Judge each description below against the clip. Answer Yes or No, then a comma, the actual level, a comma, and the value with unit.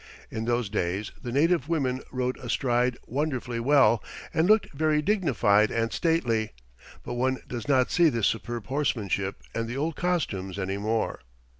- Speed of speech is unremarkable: Yes, average, 155 wpm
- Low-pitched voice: Yes, low, 125 Hz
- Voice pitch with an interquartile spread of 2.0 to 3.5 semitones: No, average, 4.7 semitones